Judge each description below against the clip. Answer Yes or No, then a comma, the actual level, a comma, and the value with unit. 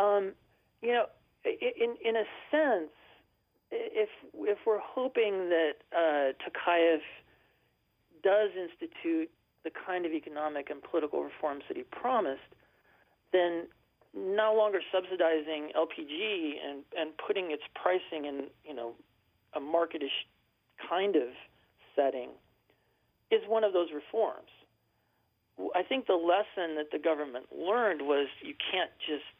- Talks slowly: Yes, slow, 125 wpm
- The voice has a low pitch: No, medium, 180 Hz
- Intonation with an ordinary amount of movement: No, wide, 6.9 semitones